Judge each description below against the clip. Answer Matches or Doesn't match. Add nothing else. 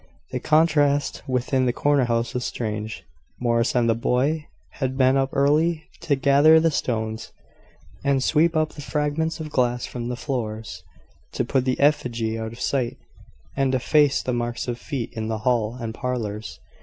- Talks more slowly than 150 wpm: Doesn't match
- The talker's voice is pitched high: Doesn't match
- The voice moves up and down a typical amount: Matches